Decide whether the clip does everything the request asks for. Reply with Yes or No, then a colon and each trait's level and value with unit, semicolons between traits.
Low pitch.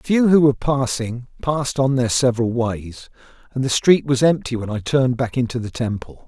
Yes: low, 125 Hz